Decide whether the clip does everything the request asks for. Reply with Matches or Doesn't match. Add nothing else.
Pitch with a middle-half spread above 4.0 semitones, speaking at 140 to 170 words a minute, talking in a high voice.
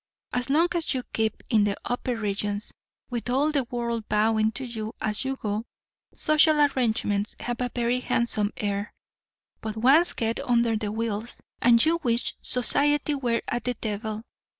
Doesn't match